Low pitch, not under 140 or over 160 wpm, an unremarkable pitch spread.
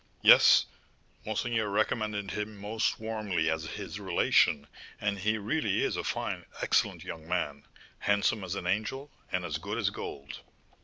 Yes: low, 100 Hz; average, 150 wpm; average, 3.4 semitones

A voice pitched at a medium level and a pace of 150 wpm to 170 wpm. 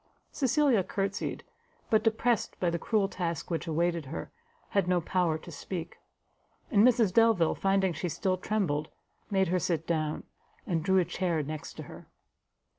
Yes: medium, 180 Hz; average, 160 wpm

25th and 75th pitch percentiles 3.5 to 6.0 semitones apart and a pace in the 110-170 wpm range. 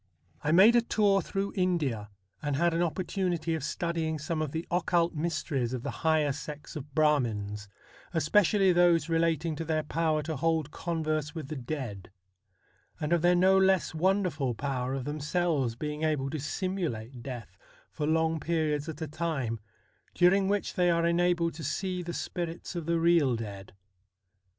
No: average, 3.1 semitones; average, 165 wpm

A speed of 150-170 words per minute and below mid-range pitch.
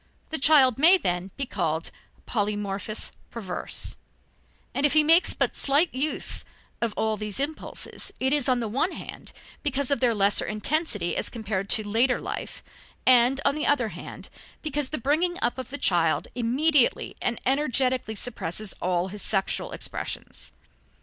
No: average, 155 wpm; high, 245 Hz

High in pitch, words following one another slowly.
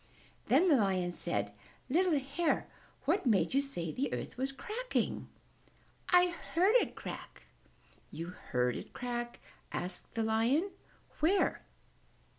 Yes: very high, 260 Hz; slow, 125 wpm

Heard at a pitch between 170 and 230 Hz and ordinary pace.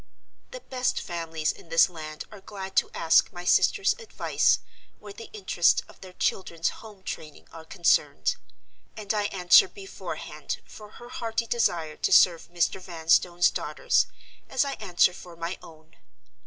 Yes: medium, 185 Hz; average, 155 wpm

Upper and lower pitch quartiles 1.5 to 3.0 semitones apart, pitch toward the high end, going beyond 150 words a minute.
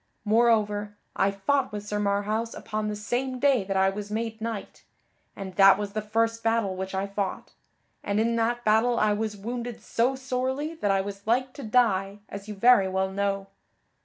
Yes: average, 2.7 semitones; high, 215 Hz; average, 190 wpm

